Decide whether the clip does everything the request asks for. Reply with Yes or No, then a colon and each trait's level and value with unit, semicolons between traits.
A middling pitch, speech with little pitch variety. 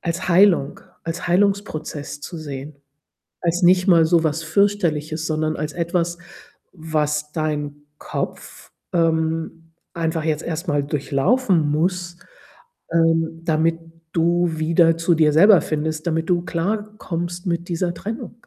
Yes: medium, 165 Hz; narrow, 2.1 semitones